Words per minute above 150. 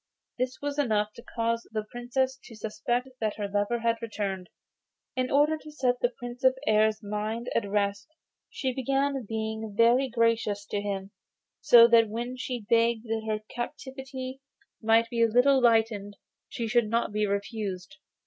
Yes: average, 170 wpm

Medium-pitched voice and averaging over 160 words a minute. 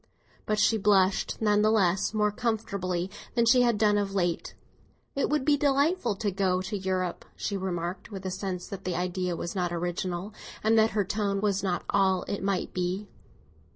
No: high, 195 Hz; average, 190 wpm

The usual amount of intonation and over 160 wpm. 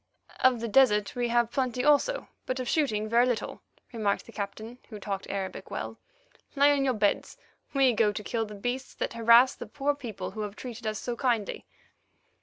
Yes: average, 3.3 semitones; average, 195 wpm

